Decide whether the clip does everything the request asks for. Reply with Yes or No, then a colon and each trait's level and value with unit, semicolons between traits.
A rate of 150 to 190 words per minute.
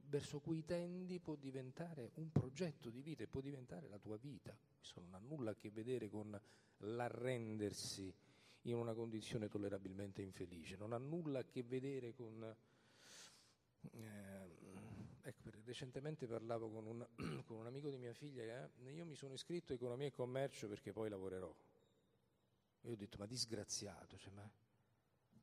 Yes: average, 165 wpm